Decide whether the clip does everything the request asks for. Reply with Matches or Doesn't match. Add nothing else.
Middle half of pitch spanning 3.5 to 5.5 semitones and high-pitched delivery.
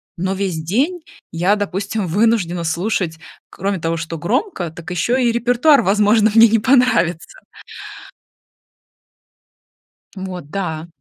Matches